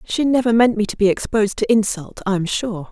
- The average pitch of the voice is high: Yes, high, 215 Hz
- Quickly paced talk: Yes, fast, 245 wpm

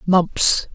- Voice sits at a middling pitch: Yes, medium, 180 Hz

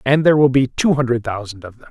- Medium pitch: No, low, 130 Hz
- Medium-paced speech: No, fast, 285 wpm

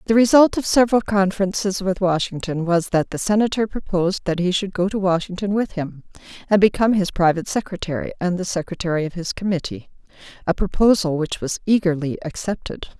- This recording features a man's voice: No, female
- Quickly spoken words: No, average, 170 wpm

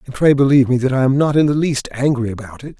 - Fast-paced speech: Yes, fast, 300 wpm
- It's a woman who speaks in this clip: No, male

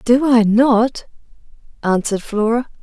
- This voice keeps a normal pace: No, slow, 105 wpm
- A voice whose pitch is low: No, high, 230 Hz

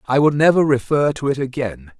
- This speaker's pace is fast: Yes, fast, 210 wpm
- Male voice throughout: Yes, male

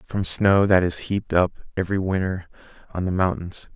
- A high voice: No, very low, 95 Hz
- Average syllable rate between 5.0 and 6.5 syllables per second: Yes, 5.2 syllables/s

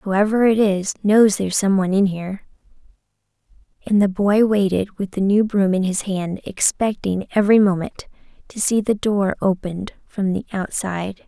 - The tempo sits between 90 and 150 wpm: No, average, 160 wpm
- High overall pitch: Yes, high, 200 Hz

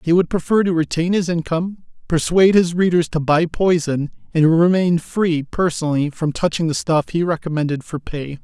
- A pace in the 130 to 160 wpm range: No, average, 180 wpm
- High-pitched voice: No, medium, 165 Hz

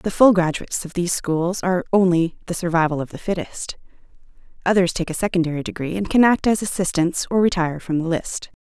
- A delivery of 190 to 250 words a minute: Yes, average, 195 wpm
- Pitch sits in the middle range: Yes, medium, 175 Hz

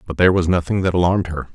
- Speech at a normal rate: No, fast, 270 wpm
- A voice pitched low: Yes, very low, 90 Hz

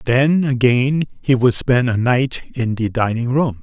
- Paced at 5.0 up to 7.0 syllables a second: No, 4.0 syllables/s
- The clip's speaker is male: Yes, male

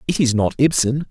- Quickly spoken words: Yes, fast, 215 wpm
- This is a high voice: No, low, 130 Hz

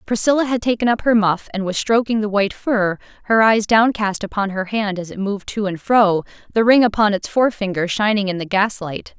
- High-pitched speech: Yes, high, 210 Hz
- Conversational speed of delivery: No, fast, 215 wpm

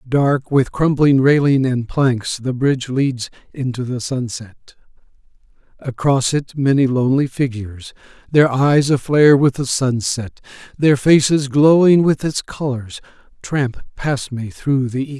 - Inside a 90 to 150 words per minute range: Yes, average, 140 wpm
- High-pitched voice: No, low, 135 Hz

